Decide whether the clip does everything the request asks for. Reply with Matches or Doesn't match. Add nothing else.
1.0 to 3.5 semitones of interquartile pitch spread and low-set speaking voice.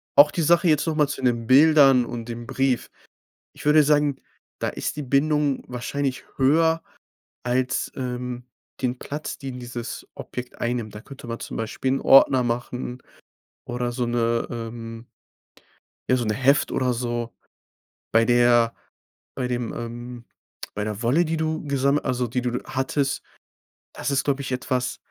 Matches